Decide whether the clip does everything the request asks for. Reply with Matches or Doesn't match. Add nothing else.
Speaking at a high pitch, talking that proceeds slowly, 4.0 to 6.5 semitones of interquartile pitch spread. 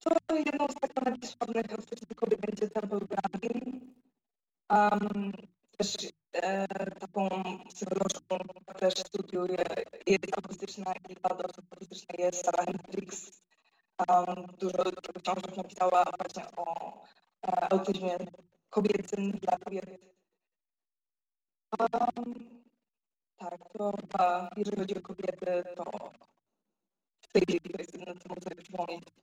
Doesn't match